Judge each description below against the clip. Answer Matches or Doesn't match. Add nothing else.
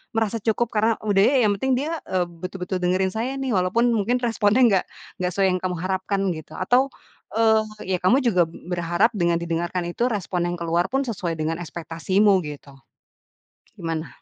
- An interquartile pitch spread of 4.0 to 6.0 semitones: Matches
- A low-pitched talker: Doesn't match